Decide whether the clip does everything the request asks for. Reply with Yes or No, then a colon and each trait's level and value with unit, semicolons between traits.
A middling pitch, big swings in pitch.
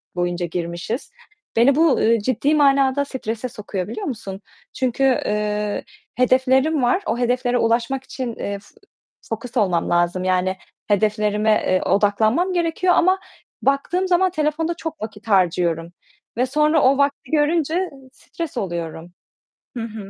No: high, 235 Hz; wide, 5.8 semitones